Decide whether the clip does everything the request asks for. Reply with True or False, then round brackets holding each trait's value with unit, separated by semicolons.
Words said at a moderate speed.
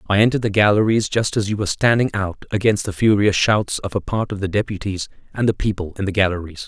False (235 wpm)